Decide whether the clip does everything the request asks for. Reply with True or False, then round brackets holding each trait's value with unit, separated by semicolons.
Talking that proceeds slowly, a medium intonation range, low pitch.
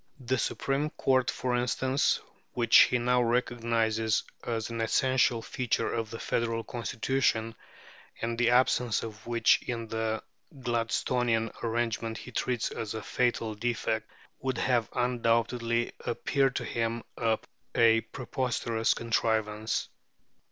False (120 wpm; 1.6 semitones; 115 Hz)